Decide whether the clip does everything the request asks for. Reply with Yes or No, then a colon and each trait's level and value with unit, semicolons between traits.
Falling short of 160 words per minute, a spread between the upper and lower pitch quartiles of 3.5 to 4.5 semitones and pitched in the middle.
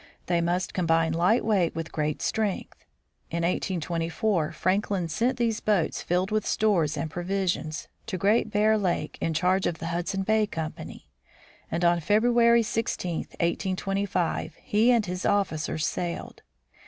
Yes: average, 140 wpm; average, 4.1 semitones; medium, 180 Hz